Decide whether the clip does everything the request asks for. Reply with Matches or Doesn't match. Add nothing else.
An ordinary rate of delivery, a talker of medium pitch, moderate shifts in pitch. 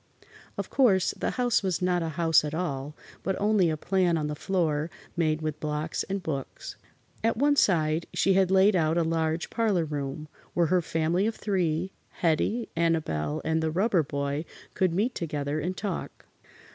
Matches